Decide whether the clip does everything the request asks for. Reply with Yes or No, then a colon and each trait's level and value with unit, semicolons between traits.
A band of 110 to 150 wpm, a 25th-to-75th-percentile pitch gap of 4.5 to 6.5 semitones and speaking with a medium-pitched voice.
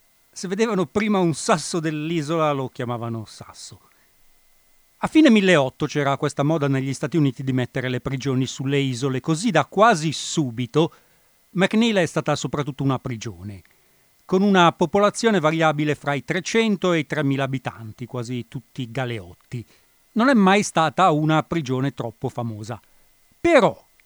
Yes: average, 140 wpm; average, 5.2 semitones; medium, 150 Hz